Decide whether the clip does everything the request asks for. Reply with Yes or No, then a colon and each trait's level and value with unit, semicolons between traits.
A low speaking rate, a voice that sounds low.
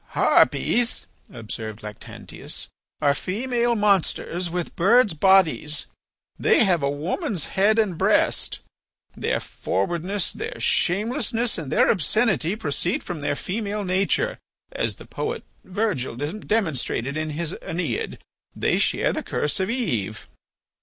No: slow, 120 wpm; medium, 185 Hz